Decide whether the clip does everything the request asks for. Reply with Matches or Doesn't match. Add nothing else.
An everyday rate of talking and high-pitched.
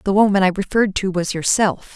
Doesn't match